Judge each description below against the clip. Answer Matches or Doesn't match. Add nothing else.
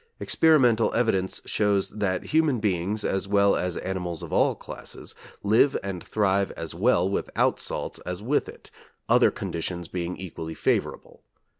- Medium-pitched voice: Doesn't match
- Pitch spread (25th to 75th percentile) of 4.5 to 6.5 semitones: Doesn't match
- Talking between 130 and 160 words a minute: Matches